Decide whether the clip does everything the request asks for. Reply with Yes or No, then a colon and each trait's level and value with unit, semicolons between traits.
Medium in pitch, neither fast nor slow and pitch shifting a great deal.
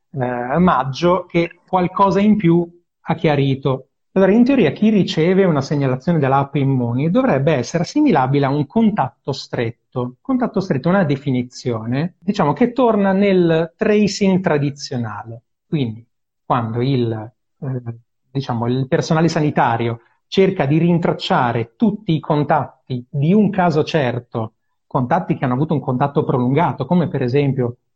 Yes: medium, 150 Hz; average, 135 wpm; wide, 5.7 semitones